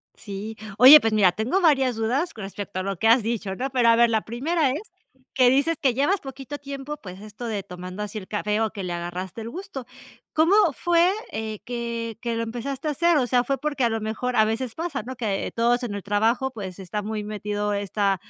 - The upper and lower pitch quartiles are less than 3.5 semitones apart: No, average, 4.3 semitones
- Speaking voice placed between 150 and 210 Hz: No, high, 230 Hz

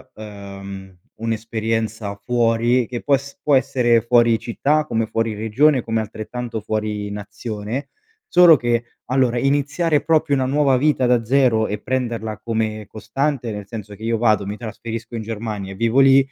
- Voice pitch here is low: Yes, low, 115 Hz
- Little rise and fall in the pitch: No, average, 3.1 semitones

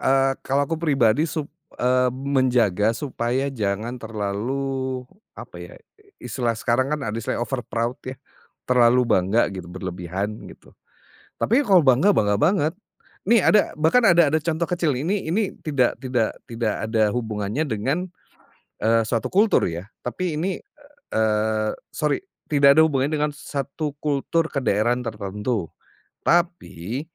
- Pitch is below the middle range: Yes, low, 130 Hz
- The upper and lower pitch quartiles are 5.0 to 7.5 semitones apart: Yes, wide, 5.5 semitones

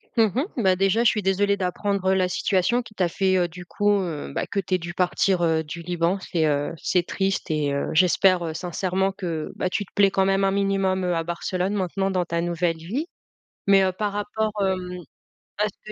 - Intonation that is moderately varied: No, narrow, 2.2 semitones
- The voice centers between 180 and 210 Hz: Yes, medium, 185 Hz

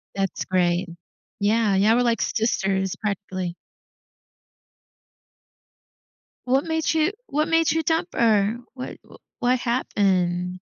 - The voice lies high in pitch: Yes, high, 215 Hz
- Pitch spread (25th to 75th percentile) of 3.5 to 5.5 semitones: Yes, average, 5.2 semitones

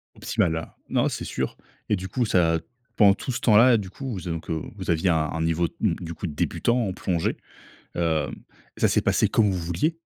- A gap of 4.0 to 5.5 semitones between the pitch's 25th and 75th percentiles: Yes, average, 4.4 semitones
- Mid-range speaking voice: No, very low, 90 Hz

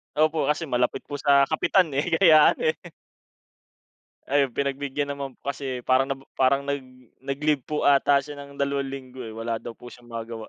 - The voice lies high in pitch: No, medium, 140 Hz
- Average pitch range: No, narrow, 1.9 semitones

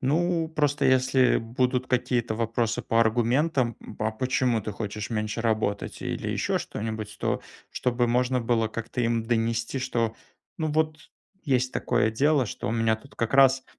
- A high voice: No, low, 120 Hz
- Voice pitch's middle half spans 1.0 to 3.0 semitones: Yes, narrow, 2.6 semitones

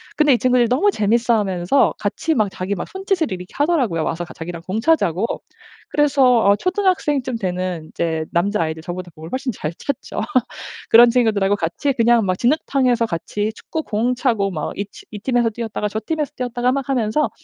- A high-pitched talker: Yes, high, 230 Hz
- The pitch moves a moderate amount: No, wide, 6.1 semitones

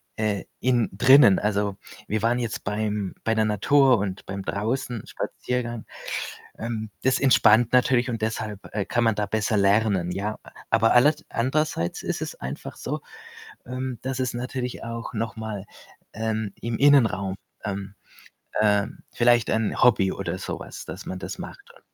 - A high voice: No, low, 110 Hz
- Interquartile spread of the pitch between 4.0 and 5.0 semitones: No, average, 3.0 semitones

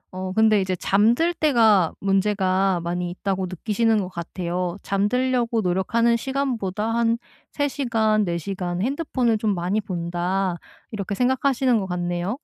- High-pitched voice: Yes, high, 200 Hz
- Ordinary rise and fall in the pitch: Yes, average, 4.2 semitones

